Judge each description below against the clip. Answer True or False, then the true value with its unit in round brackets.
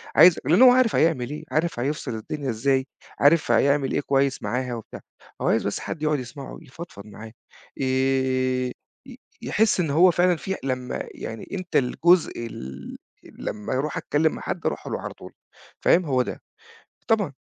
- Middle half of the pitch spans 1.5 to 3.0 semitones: False (4.3 semitones)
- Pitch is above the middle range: False (140 Hz)